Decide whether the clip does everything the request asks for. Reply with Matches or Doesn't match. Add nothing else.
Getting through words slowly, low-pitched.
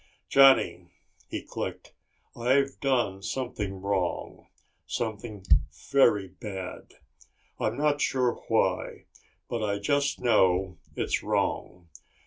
Matches